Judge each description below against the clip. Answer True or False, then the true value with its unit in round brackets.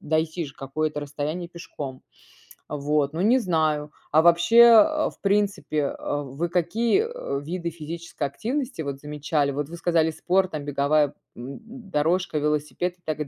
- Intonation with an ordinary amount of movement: True (3.3 semitones)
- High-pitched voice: False (155 Hz)